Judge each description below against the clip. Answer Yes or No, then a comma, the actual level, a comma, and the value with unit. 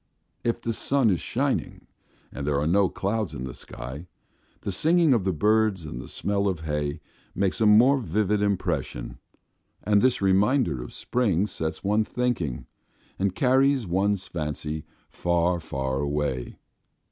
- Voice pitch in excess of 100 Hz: No, very low, 95 Hz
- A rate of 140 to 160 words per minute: Yes, average, 150 wpm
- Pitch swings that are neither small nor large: No, wide, 6.2 semitones